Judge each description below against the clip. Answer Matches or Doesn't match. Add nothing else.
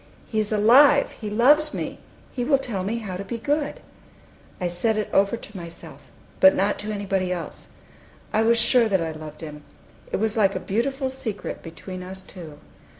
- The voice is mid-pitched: Doesn't match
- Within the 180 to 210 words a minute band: Matches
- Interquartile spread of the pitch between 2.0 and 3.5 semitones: Doesn't match